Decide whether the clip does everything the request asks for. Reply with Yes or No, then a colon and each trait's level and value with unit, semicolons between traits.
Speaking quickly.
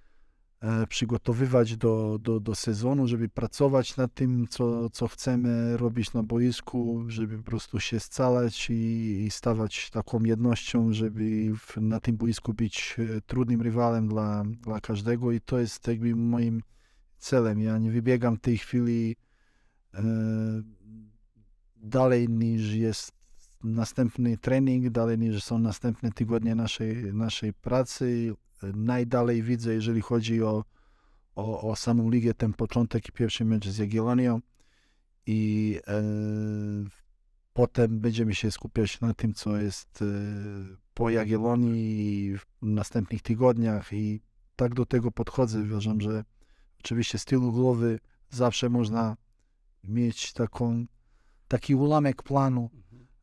No: average, 125 wpm